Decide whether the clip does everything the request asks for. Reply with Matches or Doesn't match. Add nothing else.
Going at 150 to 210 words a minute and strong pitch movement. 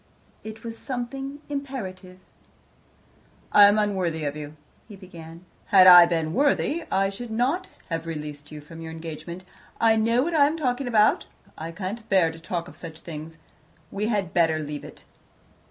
Matches